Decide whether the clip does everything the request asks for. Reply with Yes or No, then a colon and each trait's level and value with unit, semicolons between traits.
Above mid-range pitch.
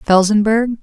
Yes: high, 215 Hz